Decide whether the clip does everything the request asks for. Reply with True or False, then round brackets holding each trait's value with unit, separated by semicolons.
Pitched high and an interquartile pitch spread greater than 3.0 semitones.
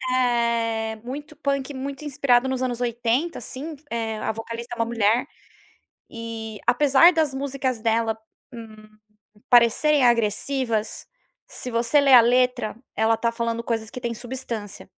False (240 Hz; 2.5 semitones)